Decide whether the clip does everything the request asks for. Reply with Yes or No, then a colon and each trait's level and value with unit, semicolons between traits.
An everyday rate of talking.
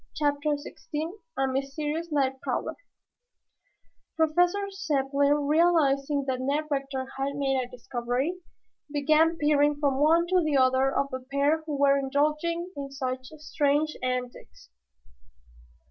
No: slow, 125 wpm